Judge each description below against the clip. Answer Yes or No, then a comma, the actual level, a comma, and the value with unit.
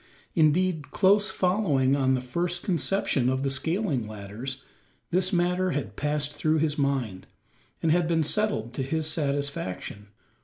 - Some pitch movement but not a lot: Yes, average, 5.0 semitones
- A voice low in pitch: No, medium, 150 Hz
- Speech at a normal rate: Yes, average, 145 wpm